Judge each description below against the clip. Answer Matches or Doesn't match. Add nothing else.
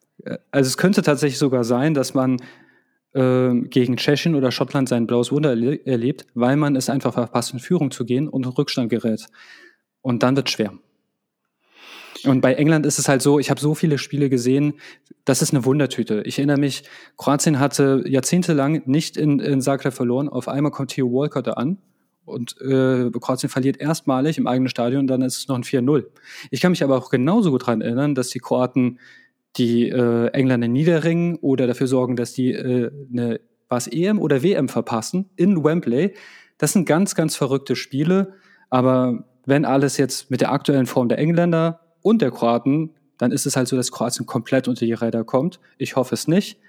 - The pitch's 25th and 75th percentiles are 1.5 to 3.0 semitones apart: Matches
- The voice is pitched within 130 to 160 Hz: Matches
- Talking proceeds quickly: Matches